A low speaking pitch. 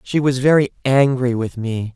Yes: low, 130 Hz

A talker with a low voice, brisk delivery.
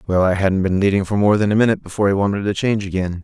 Yes: low, 100 Hz; fast, 295 wpm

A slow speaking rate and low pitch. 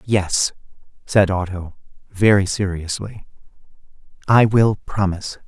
Yes: slow, 90 wpm; low, 100 Hz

